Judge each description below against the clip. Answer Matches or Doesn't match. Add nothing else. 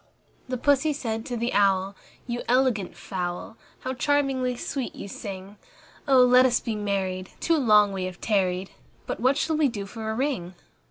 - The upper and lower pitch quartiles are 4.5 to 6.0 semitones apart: Matches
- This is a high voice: Matches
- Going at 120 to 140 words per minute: Doesn't match